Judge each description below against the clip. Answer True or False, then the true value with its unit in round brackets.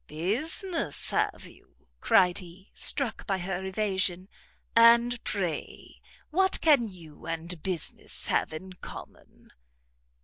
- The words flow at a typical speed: False (110 wpm)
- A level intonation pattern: False (5.0 semitones)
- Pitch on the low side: False (190 Hz)